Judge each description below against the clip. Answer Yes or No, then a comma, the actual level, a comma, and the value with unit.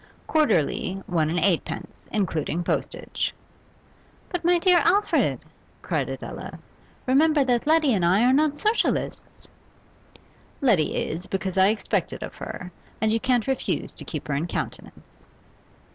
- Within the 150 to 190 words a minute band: No, average, 140 wpm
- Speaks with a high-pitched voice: Yes, high, 225 Hz